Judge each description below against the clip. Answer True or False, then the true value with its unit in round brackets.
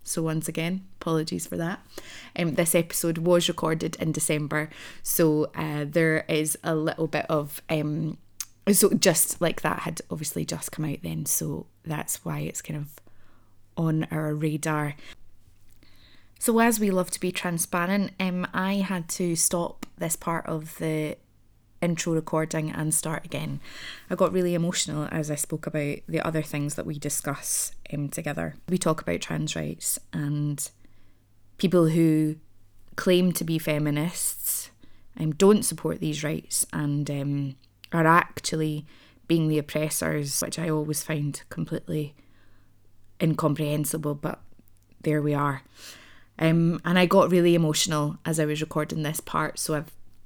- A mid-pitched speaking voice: True (155 Hz)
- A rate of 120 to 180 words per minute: True (155 wpm)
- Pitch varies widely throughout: False (2.5 semitones)